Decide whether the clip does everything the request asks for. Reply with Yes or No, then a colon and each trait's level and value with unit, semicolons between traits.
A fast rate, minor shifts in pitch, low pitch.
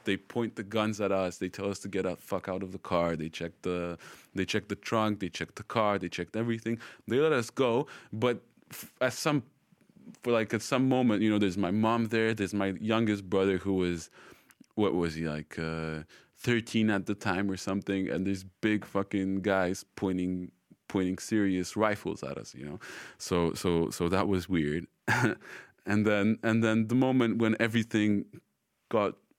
No: fast, 195 wpm; average, 3.3 semitones; low, 100 Hz